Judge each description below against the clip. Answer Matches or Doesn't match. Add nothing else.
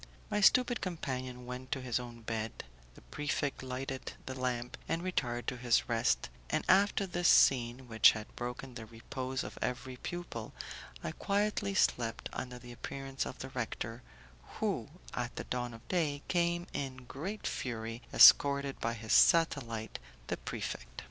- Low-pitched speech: Matches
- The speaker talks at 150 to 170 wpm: Matches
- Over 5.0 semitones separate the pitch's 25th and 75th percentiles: Doesn't match